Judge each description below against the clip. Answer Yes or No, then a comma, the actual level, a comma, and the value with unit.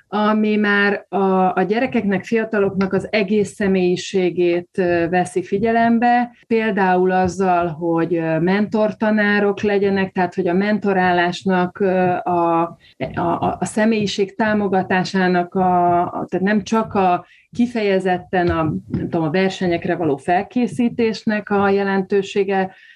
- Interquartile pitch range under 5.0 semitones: Yes, average, 2.8 semitones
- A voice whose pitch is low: No, high, 190 Hz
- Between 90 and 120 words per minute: Yes, slow, 105 wpm